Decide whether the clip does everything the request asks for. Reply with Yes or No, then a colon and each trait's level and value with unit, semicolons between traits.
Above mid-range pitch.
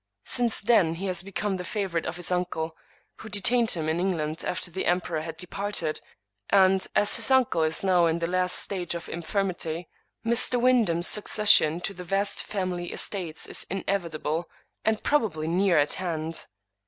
No: medium, 180 Hz